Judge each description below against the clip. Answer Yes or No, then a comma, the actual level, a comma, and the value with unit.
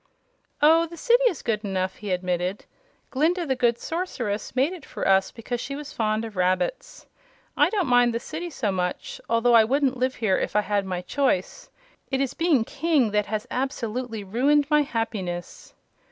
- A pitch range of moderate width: No, wide, 5.8 semitones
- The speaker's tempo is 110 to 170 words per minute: No, average, 180 wpm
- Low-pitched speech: No, high, 240 Hz